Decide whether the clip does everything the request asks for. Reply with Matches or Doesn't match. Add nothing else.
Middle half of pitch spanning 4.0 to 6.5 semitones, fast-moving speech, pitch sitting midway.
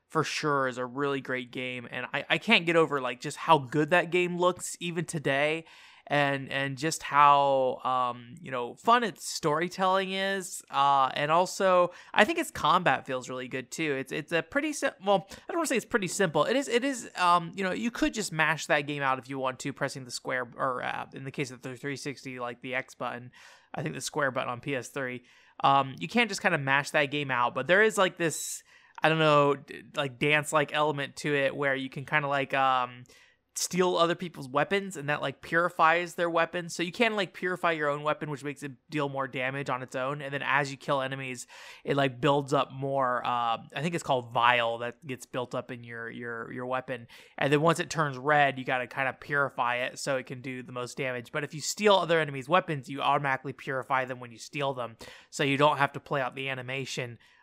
Matches